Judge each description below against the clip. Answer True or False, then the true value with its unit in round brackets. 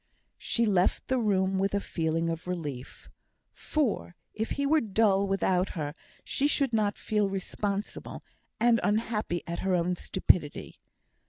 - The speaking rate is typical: True (145 wpm)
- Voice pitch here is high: True (195 Hz)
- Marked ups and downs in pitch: False (3.7 semitones)